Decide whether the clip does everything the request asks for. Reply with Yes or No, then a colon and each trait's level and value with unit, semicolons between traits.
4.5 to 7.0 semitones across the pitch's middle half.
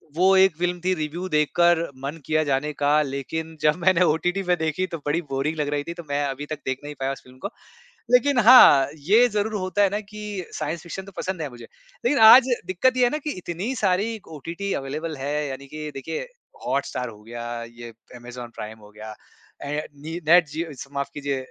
Yes: average, 5.1 semitones